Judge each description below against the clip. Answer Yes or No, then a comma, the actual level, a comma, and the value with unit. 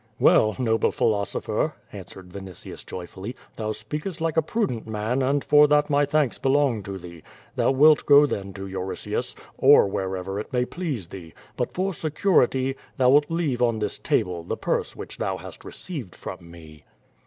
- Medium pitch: No, low, 120 Hz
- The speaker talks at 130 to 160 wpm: No, average, 170 wpm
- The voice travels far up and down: Yes, wide, 7.2 semitones